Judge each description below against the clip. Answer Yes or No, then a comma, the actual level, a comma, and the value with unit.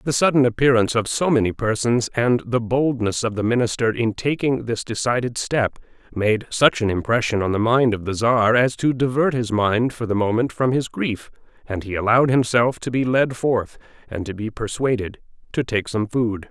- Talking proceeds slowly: No, average, 200 wpm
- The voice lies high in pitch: No, low, 120 Hz